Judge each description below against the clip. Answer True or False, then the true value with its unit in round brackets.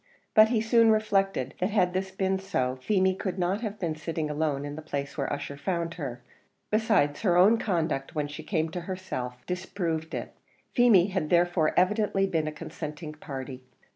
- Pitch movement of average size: True (4.3 semitones)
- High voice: False (175 Hz)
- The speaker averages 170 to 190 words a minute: True (180 wpm)